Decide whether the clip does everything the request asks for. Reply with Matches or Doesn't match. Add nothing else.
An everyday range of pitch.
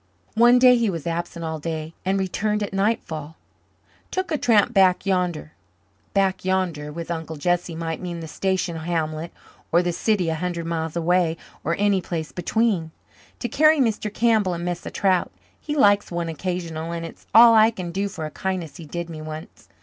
Matches